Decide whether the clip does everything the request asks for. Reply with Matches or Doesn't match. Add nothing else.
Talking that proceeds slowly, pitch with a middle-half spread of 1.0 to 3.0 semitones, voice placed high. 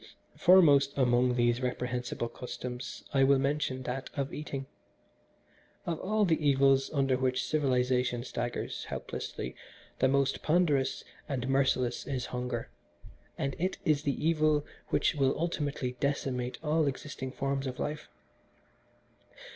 Doesn't match